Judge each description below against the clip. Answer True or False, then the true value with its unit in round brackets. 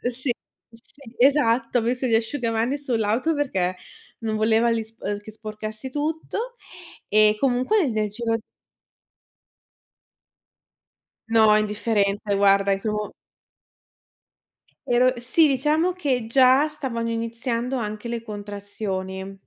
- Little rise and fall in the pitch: False (3.4 semitones)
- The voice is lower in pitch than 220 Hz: False (230 Hz)